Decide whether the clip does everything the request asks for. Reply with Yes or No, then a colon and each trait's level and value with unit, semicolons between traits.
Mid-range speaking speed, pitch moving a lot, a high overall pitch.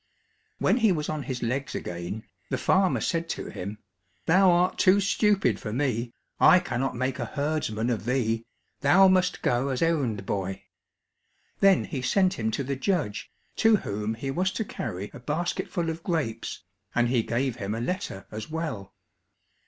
No: average, 170 wpm; wide, 7.5 semitones; low, 135 Hz